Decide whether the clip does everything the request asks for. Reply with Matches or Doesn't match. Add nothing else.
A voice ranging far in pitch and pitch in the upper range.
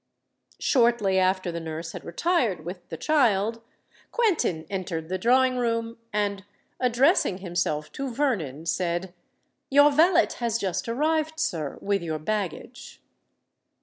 Matches